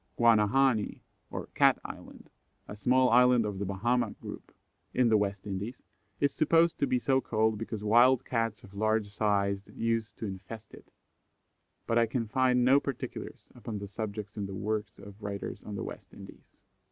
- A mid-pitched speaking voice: No, low, 110 Hz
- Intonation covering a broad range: No, average, 3.4 semitones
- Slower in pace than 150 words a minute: No, average, 175 wpm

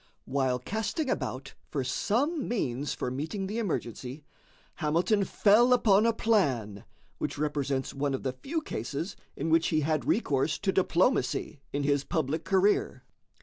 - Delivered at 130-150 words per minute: Yes, average, 145 wpm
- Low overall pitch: No, medium, 155 Hz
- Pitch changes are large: Yes, wide, 7.3 semitones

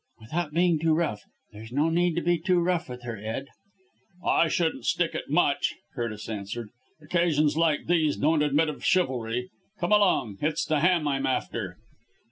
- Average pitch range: No, wide, 6.0 semitones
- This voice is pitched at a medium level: Yes, medium, 150 Hz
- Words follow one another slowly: No, average, 170 wpm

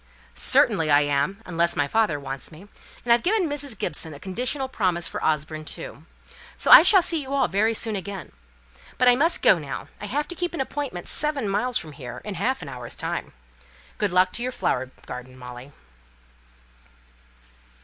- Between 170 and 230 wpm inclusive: Yes, average, 185 wpm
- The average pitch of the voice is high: Yes, high, 200 Hz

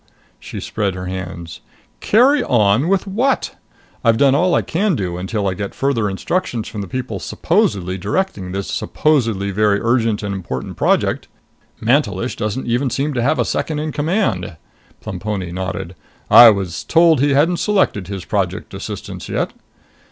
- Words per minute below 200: Yes, average, 160 wpm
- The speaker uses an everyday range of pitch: No, wide, 7.6 semitones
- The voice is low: Yes, low, 110 Hz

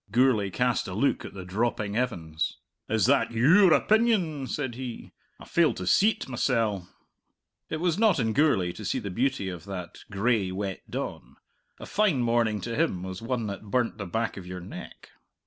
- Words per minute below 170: No, average, 180 wpm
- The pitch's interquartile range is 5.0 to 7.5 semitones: Yes, wide, 5.5 semitones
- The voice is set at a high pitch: No, low, 115 Hz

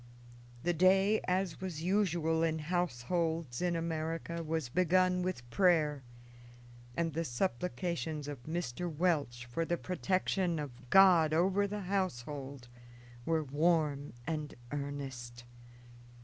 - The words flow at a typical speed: No, slow, 115 wpm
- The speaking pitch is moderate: Yes, medium, 165 Hz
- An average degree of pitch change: Yes, average, 3.8 semitones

